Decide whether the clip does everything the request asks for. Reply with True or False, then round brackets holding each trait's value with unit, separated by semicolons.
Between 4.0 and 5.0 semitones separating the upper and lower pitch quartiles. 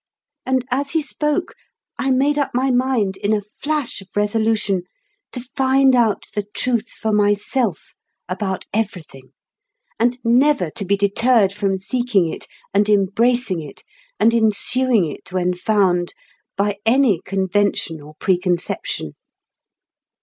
True (4.6 semitones)